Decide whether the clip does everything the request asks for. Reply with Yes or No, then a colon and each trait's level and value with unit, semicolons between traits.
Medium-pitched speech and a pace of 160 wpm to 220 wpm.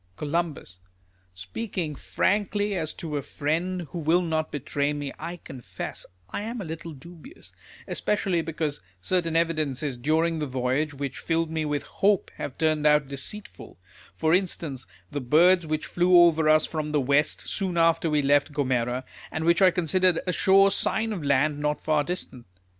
Yes: medium, 155 Hz; average, 165 wpm